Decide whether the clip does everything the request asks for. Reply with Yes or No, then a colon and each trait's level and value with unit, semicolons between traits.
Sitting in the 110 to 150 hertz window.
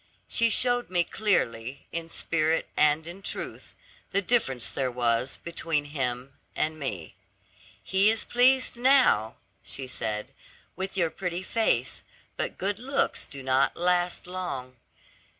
No: medium, 165 Hz